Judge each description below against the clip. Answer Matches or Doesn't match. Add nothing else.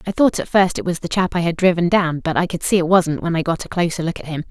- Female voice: Matches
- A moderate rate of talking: Doesn't match